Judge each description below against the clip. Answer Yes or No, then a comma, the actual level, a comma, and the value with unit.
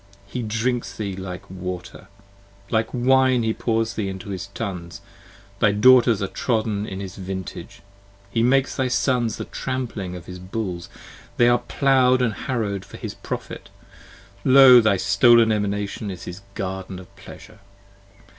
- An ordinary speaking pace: Yes, average, 155 wpm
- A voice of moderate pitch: No, low, 110 Hz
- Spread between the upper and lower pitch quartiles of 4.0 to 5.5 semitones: Yes, average, 4.3 semitones